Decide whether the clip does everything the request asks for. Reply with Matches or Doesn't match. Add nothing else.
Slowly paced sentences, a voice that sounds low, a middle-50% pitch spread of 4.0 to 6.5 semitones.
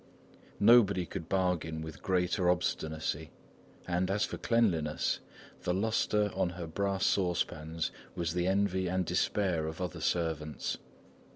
Doesn't match